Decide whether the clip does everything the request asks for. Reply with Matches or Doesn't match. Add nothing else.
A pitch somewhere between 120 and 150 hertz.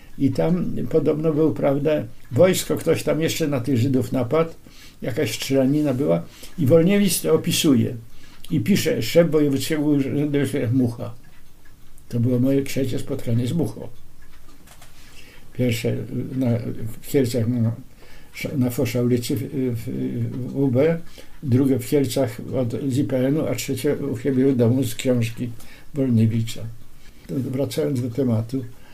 Matches